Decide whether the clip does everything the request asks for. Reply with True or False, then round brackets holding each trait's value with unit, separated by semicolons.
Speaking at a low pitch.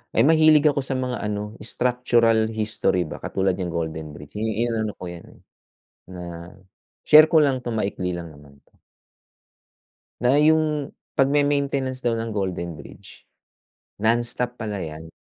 True (110 Hz)